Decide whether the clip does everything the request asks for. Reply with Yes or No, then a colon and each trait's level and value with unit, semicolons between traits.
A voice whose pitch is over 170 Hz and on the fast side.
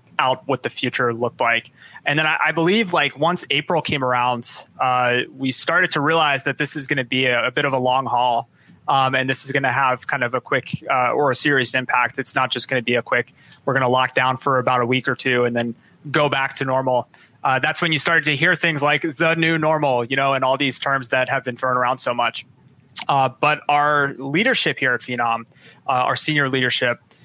No: low, 135 Hz; fast, 245 wpm